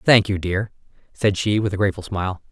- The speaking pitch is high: No, low, 100 Hz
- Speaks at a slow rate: No, fast, 215 wpm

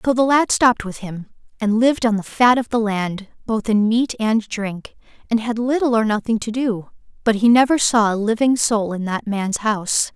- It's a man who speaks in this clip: No, female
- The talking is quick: Yes, fast, 220 wpm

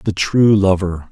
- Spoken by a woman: No, male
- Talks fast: No, average, 160 wpm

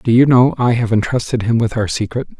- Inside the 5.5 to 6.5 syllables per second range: Yes, 5.9 syllables/s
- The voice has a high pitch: No, low, 120 Hz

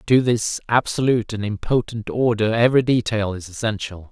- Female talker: No, male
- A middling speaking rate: Yes, average, 145 wpm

